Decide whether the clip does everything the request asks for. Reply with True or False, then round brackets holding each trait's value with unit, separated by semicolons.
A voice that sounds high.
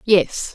True (195 Hz)